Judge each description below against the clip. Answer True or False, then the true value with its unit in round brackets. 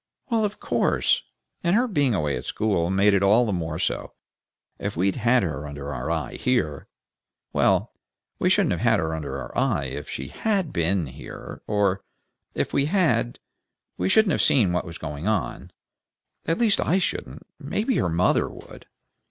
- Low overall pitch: True (95 Hz)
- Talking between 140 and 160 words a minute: False (175 wpm)